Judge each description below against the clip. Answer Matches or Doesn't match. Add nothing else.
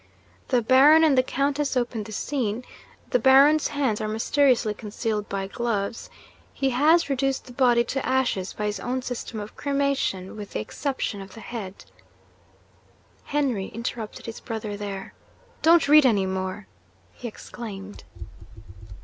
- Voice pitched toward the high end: Matches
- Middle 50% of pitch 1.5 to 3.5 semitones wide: Doesn't match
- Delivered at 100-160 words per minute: Matches